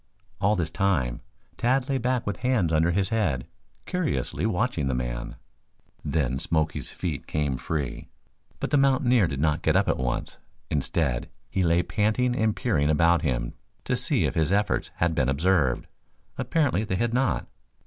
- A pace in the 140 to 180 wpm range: Yes, average, 165 wpm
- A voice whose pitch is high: No, very low, 85 Hz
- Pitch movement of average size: No, wide, 7.7 semitones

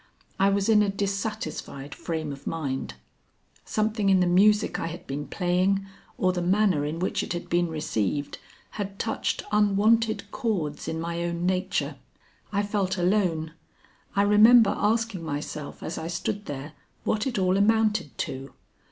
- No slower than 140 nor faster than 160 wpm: Yes, average, 155 wpm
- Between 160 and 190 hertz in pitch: Yes, medium, 185 Hz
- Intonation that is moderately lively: Yes, average, 4.3 semitones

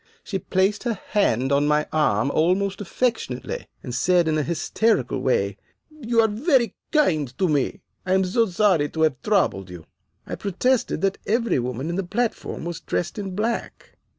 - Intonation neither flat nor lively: No, wide, 6.6 semitones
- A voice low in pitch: No, medium, 185 Hz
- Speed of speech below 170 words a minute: No, average, 175 wpm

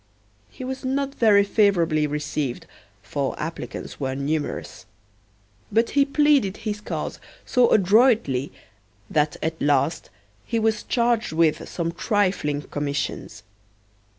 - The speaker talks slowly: Yes, slow, 115 wpm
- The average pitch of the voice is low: No, medium, 185 Hz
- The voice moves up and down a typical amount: No, wide, 7.5 semitones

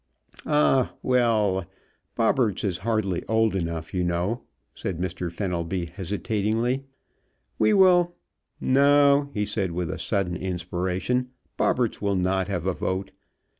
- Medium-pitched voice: No, low, 100 Hz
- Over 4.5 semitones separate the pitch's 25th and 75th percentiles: Yes, average, 5.3 semitones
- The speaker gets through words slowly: Yes, slow, 120 wpm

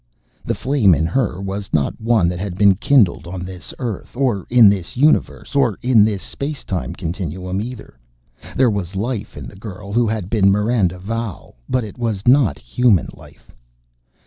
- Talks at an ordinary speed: Yes, average, 175 wpm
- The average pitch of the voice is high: No, low, 100 Hz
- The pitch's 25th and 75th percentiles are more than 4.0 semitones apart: Yes, average, 4.6 semitones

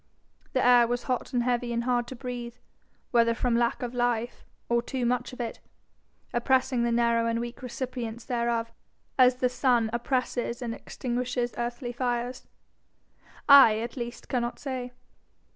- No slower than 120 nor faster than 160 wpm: Yes, average, 155 wpm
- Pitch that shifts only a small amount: Yes, narrow, 1.0 semitones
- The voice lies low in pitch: No, high, 240 Hz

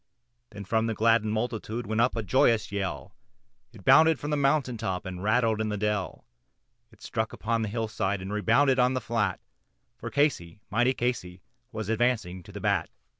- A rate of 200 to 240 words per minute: No, average, 180 wpm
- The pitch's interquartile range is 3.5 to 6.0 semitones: No, average, 3.1 semitones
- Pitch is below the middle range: Yes, low, 110 Hz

